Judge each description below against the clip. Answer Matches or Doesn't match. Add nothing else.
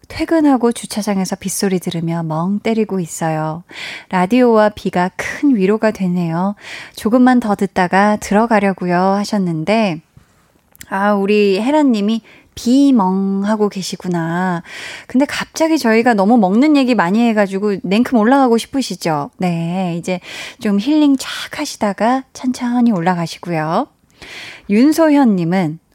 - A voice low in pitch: Doesn't match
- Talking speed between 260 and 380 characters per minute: Matches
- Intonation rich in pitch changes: Doesn't match